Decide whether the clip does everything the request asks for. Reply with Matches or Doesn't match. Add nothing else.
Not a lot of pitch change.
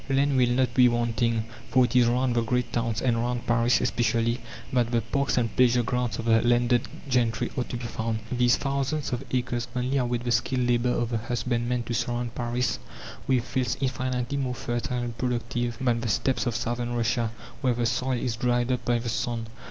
Matches